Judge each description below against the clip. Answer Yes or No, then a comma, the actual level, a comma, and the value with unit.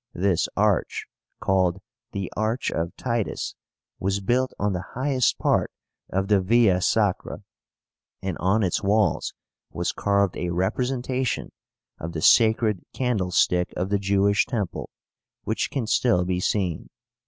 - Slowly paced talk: Yes, slow, 130 wpm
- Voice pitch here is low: Yes, low, 100 Hz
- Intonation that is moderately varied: Yes, average, 3.7 semitones